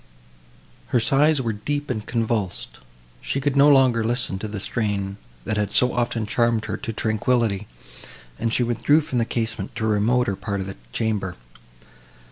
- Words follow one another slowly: No, average, 170 wpm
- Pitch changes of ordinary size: Yes, average, 3.0 semitones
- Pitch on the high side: No, low, 115 Hz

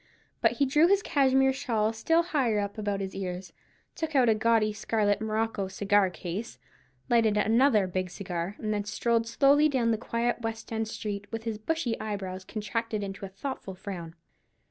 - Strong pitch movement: No, average, 3.0 semitones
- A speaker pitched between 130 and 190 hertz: No, high, 220 Hz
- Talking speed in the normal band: Yes, average, 175 wpm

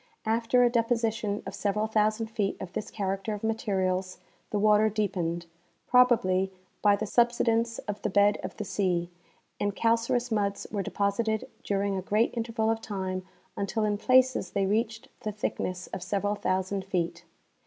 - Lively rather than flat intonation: No, narrow, 2.5 semitones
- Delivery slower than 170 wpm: Yes, average, 160 wpm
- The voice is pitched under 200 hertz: No, high, 210 Hz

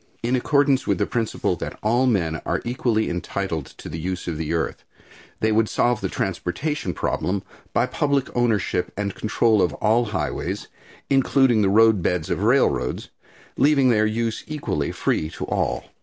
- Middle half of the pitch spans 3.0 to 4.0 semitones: No, average, 5.2 semitones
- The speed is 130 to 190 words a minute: Yes, average, 160 wpm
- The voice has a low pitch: Yes, low, 110 Hz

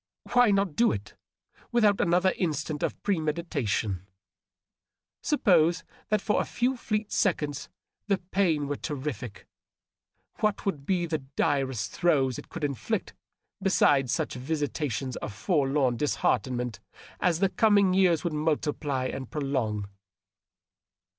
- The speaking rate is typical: No, slow, 120 wpm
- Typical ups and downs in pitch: No, wide, 6.0 semitones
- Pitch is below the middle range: No, medium, 150 Hz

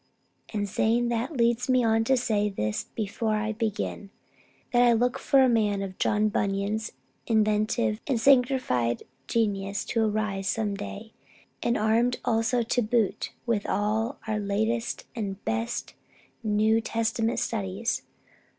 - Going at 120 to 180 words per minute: Yes, average, 140 wpm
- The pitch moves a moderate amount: No, narrow, 2.3 semitones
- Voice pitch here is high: Yes, high, 220 Hz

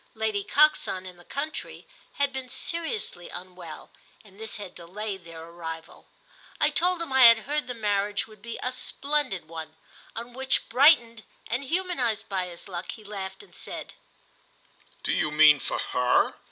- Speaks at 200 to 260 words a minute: No, average, 165 wpm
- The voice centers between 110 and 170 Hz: No, high, 215 Hz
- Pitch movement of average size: No, wide, 6.8 semitones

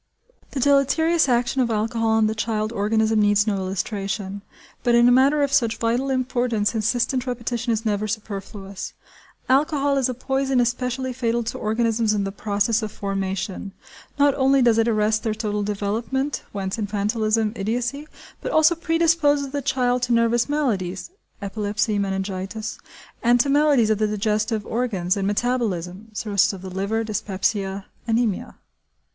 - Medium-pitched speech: No, high, 225 Hz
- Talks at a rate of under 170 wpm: Yes, average, 155 wpm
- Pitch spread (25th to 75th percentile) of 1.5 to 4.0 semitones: Yes, average, 3.5 semitones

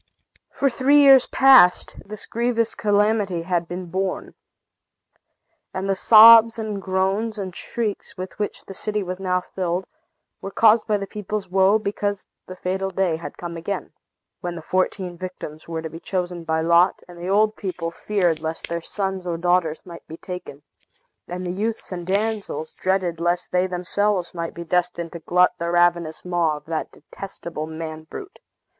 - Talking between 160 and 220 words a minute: Yes, average, 170 wpm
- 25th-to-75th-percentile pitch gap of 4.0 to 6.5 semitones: No, average, 3.1 semitones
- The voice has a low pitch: No, medium, 185 Hz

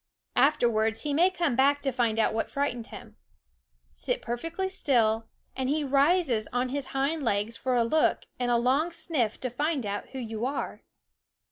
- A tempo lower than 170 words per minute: No, average, 175 wpm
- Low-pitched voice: No, very high, 260 Hz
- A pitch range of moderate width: Yes, average, 4.3 semitones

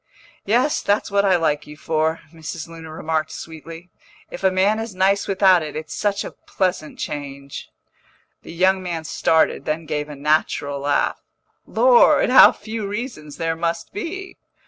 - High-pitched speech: No, medium, 165 Hz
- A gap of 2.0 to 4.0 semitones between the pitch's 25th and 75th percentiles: No, average, 4.4 semitones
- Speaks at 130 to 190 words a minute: Yes, average, 160 wpm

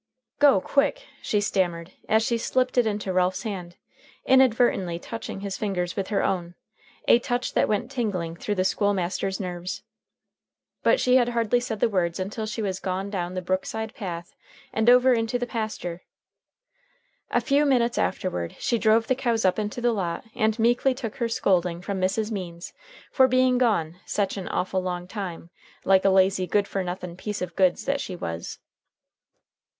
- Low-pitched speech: No, high, 205 Hz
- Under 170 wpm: No, average, 175 wpm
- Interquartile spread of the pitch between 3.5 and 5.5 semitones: Yes, average, 4.4 semitones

